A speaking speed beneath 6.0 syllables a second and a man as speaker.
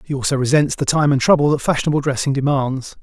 No: 6.5 syllables/s; male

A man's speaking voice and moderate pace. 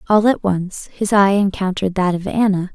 No: female; average, 195 wpm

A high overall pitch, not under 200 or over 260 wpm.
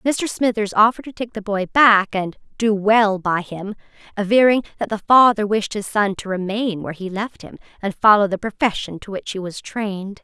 Yes: high, 205 Hz; fast, 205 wpm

